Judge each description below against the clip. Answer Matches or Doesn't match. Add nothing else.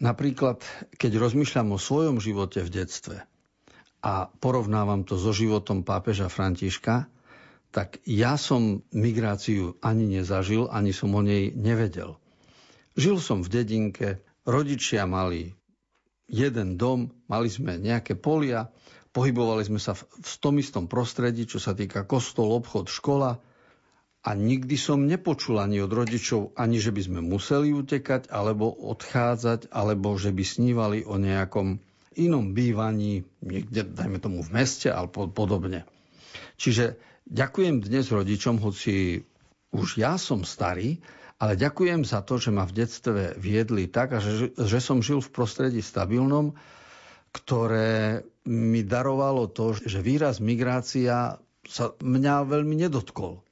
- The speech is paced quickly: Doesn't match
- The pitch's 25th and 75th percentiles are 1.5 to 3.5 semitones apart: Doesn't match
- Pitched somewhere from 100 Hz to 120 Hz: Matches